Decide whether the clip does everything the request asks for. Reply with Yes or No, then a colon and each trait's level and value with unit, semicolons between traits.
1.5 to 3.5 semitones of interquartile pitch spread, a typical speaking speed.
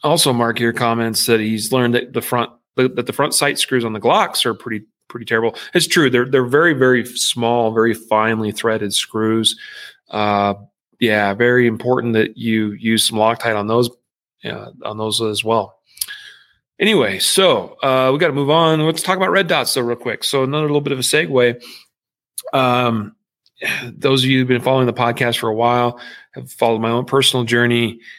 Yes: narrow, 2.4 semitones; average, 190 wpm